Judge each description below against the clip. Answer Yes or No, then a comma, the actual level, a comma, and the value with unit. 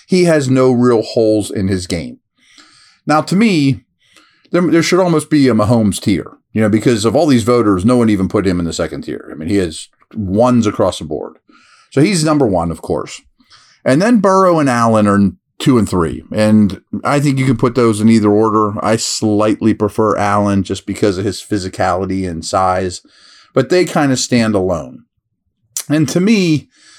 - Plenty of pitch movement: Yes, wide, 6.0 semitones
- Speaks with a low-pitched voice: Yes, low, 110 Hz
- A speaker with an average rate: Yes, average, 195 wpm